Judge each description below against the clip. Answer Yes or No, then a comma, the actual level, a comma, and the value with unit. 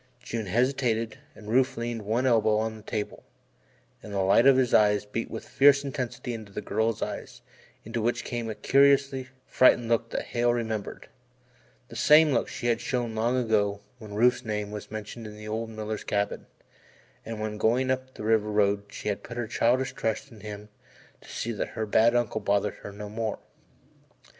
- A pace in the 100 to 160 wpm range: No, average, 190 wpm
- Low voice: Yes, low, 115 Hz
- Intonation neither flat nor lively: No, narrow, 2.3 semitones